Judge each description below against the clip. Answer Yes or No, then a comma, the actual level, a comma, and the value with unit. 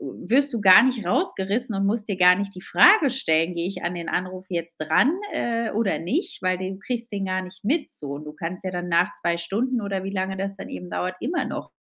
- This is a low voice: No, high, 190 Hz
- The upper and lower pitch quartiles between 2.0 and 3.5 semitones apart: No, average, 4.3 semitones